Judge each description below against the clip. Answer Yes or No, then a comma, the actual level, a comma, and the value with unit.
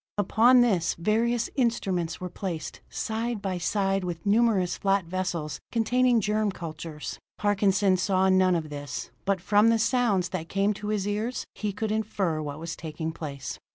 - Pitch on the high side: Yes, high, 195 Hz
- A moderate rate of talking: Yes, average, 160 wpm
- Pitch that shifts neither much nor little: Yes, average, 4.1 semitones